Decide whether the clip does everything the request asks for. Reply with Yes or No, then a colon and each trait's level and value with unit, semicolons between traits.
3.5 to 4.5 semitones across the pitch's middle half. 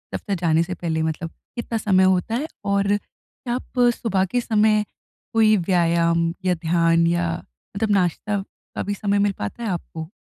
Yes: average, 3.9 semitones